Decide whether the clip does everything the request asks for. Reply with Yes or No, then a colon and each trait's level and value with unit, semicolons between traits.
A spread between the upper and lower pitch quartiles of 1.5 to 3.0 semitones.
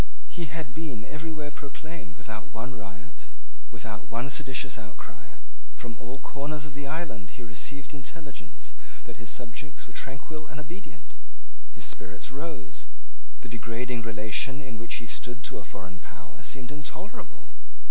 No: average, 5.0 semitones